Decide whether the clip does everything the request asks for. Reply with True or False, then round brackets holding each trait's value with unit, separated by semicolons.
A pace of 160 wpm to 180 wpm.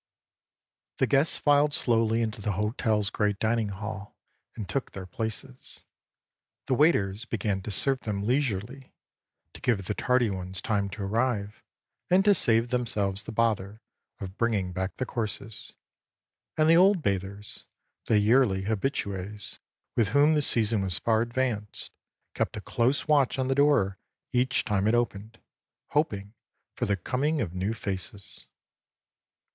False (145 wpm)